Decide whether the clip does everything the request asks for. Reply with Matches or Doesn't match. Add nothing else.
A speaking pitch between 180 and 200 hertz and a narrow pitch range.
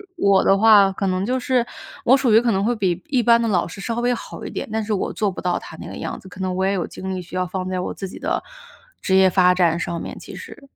Doesn't match